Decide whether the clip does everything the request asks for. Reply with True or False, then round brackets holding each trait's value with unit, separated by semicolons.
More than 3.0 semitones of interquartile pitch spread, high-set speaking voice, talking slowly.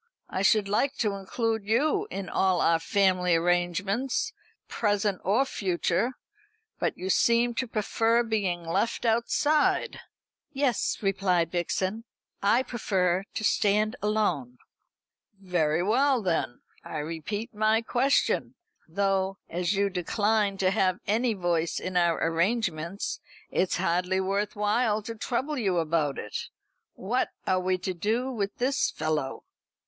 True (4.2 semitones; 200 Hz; 130 wpm)